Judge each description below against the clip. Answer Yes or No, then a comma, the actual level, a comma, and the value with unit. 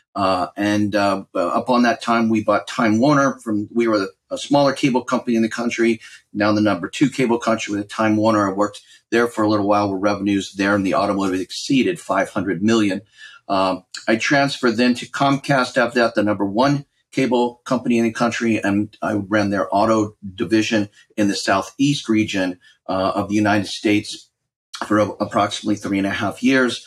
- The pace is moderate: Yes, average, 195 wpm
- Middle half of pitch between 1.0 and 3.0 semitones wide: Yes, narrow, 2.6 semitones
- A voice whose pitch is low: Yes, low, 110 Hz